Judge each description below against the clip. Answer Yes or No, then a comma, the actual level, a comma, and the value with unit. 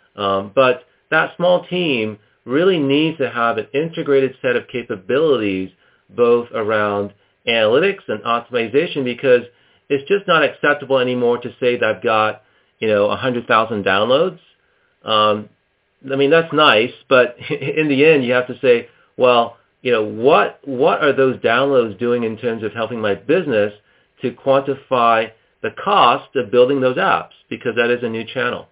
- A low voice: Yes, low, 120 Hz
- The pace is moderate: Yes, average, 160 wpm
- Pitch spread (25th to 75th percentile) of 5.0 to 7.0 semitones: No, average, 3.9 semitones